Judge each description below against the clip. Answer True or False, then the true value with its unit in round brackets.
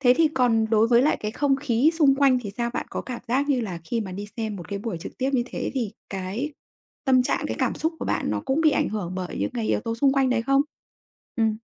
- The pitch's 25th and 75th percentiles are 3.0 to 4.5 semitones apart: True (4.0 semitones)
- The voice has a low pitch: False (240 Hz)